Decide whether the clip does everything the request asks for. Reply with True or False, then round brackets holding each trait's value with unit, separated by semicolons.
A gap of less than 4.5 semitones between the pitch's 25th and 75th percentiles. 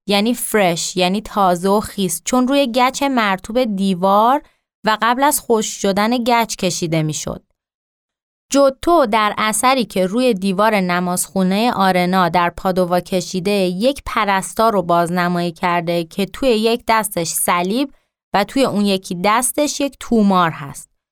False (4.8 semitones)